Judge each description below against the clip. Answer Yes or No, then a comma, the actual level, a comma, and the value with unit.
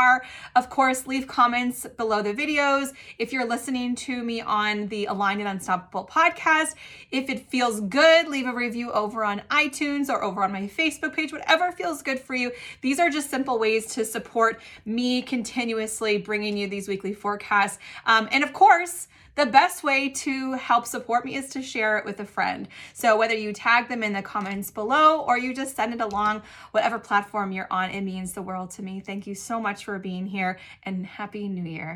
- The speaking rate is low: No, average, 200 wpm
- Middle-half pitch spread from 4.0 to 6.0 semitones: Yes, average, 4.5 semitones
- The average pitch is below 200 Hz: No, high, 230 Hz